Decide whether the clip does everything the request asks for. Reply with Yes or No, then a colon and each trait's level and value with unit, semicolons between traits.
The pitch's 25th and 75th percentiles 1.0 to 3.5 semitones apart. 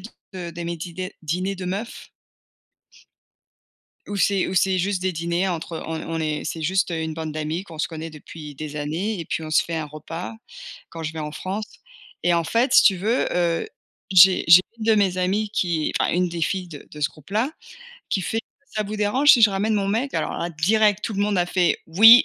No: average, 3.9 semitones